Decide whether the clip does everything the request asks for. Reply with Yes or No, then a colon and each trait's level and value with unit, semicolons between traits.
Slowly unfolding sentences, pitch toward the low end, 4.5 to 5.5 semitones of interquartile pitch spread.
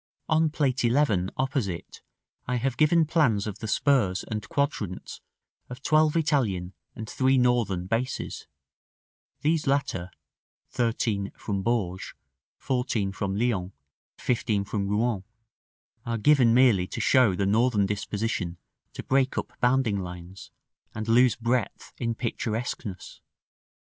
Yes: slow, 125 wpm; low, 115 Hz; average, 4.8 semitones